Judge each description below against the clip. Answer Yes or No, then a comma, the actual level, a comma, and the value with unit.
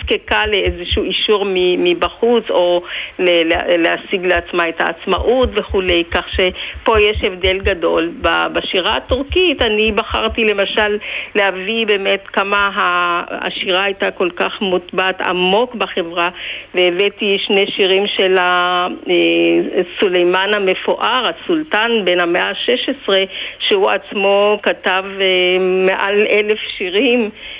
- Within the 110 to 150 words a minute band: No, slow, 100 wpm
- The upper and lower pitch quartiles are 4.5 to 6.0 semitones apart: No, average, 2.8 semitones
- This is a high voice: Yes, high, 195 Hz